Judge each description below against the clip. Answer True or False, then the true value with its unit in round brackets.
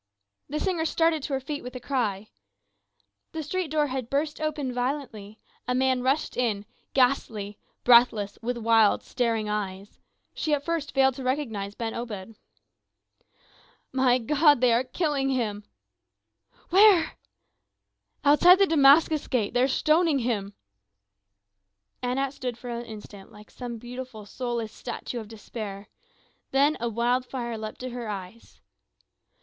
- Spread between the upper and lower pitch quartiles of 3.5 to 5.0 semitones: True (4.1 semitones)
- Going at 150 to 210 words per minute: False (140 wpm)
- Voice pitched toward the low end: False (250 Hz)